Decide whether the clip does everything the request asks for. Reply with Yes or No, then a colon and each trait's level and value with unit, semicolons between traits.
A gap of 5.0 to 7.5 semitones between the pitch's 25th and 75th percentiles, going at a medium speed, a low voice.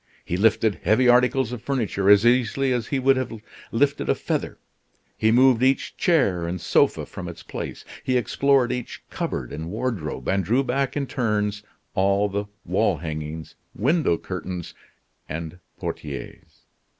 Yes: average, 5.3 semitones; average, 150 wpm; low, 110 Hz